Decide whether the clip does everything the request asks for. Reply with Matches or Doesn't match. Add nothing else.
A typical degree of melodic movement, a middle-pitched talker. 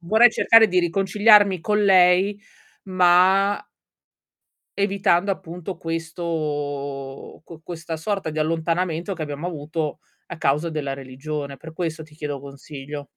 Matches